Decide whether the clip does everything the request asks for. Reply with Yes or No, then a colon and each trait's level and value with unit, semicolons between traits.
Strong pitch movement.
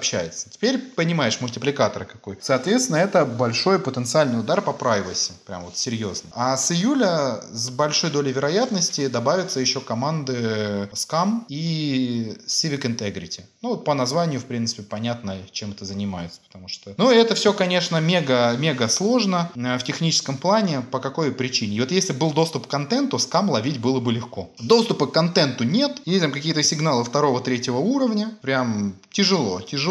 Yes: wide, 6.8 semitones